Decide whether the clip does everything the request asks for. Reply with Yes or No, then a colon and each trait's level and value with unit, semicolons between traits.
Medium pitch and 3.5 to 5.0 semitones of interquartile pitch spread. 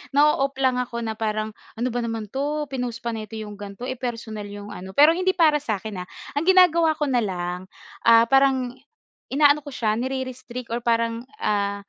No: high, 235 Hz; average, 4.1 semitones